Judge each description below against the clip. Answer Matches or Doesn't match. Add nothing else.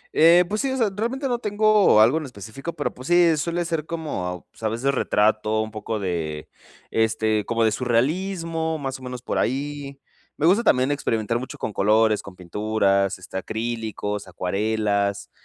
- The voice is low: Matches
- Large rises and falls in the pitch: Matches